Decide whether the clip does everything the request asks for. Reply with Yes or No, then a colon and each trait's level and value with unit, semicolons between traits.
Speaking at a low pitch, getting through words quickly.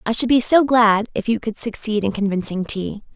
No: high, 220 Hz; fast, 230 wpm